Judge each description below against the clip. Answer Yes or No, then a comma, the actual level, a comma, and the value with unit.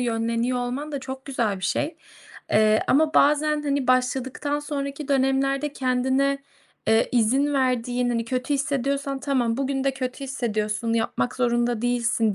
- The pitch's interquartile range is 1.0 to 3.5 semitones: Yes, average, 2.7 semitones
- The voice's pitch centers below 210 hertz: No, very high, 260 Hz